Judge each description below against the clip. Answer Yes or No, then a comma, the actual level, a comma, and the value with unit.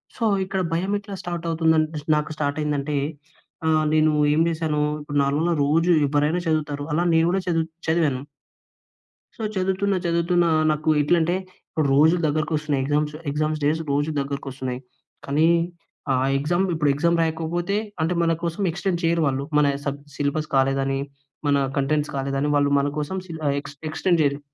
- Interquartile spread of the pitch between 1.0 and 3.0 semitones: Yes, average, 2.7 semitones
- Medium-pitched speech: Yes, medium, 155 Hz